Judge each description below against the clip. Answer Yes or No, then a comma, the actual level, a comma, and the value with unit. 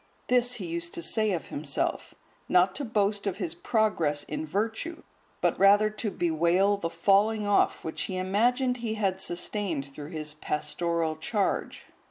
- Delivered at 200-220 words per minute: No, average, 160 wpm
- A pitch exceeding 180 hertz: Yes, high, 190 Hz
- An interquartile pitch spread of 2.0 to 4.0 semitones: No, average, 4.5 semitones